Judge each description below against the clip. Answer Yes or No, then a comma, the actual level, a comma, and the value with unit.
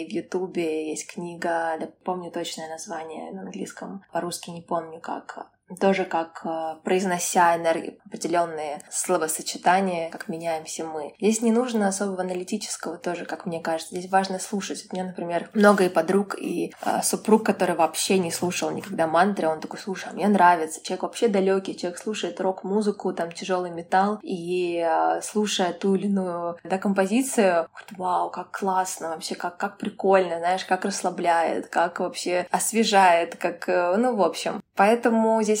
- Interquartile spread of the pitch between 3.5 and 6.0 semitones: No, average, 2.8 semitones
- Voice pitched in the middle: Yes, medium, 180 Hz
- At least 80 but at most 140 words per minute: No, fast, 160 wpm